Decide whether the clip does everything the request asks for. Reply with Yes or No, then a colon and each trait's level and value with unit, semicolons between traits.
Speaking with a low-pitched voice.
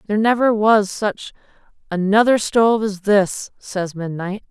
No: high, 205 Hz